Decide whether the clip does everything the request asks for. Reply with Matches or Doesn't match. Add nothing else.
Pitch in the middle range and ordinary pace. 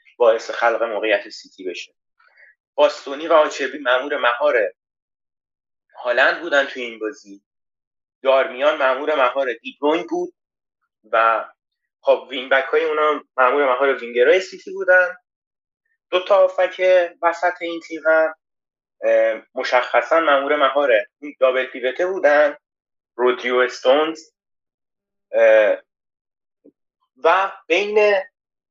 Doesn't match